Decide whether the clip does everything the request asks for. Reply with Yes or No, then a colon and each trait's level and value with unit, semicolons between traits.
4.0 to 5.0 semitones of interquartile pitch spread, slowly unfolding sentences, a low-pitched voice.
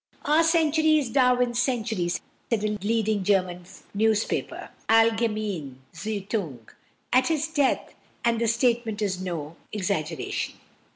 No: average, 4.6 semitones; slow, 115 wpm; high, 220 Hz